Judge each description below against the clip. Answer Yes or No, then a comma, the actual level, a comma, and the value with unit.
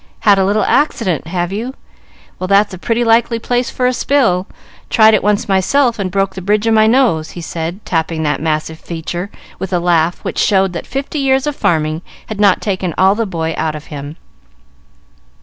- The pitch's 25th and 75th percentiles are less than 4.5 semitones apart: No, average, 5.0 semitones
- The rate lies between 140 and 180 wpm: No, average, 200 wpm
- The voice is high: Yes, high, 195 Hz